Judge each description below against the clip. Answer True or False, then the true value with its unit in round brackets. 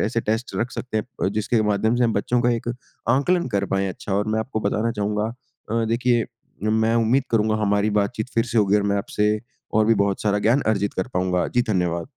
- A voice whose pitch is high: False (110 Hz)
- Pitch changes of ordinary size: False (2.3 semitones)